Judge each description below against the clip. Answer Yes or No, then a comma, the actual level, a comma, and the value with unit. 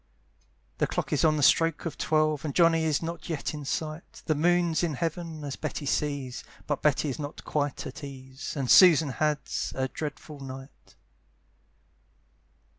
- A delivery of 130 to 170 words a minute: Yes, average, 165 wpm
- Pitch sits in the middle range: Yes, medium, 150 Hz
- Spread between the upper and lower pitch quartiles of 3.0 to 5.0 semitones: No, narrow, 2.5 semitones